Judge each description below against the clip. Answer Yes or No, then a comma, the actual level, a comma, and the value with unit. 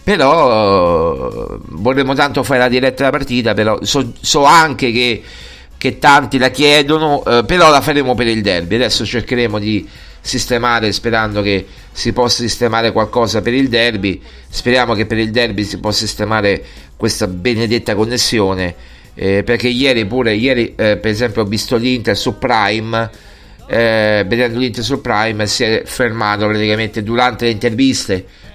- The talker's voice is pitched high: No, low, 115 Hz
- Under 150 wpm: No, average, 155 wpm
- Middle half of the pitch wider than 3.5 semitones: No, average, 3.1 semitones